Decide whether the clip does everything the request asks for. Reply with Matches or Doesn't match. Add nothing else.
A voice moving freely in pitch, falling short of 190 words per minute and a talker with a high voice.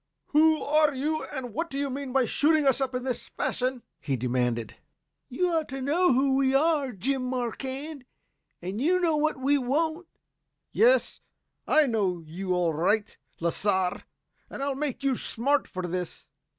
Matches